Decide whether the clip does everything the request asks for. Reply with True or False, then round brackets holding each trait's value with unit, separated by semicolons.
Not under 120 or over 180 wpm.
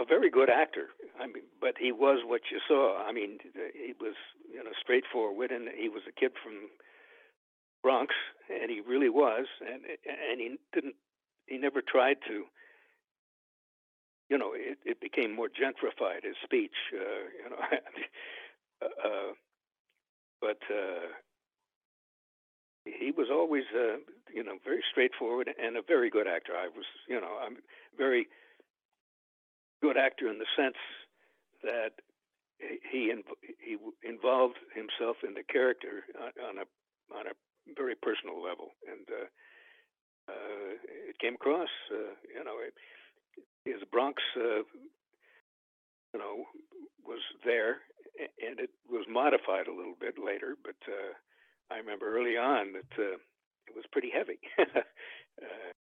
True (140 wpm)